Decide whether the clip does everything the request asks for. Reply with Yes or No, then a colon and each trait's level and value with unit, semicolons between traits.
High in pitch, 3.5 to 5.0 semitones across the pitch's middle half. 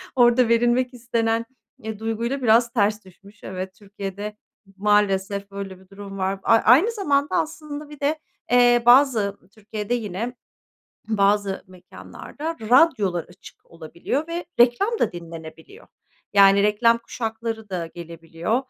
Yes: high, 220 Hz; average, 3.8 semitones